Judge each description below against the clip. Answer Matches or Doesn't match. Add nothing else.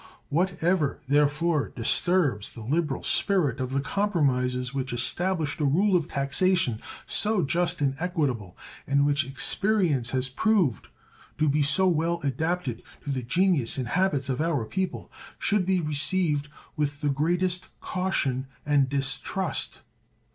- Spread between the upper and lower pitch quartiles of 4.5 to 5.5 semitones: Matches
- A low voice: Doesn't match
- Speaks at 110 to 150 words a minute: Matches